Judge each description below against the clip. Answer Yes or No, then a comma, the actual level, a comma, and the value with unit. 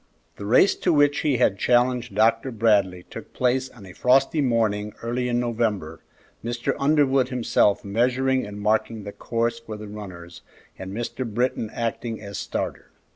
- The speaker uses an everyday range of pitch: Yes, average, 3.4 semitones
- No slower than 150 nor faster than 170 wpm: Yes, average, 160 wpm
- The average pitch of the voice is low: Yes, low, 115 Hz